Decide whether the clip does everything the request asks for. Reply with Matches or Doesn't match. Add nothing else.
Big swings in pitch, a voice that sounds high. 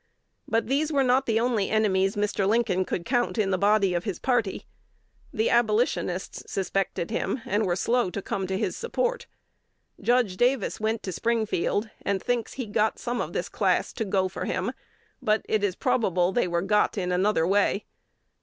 Doesn't match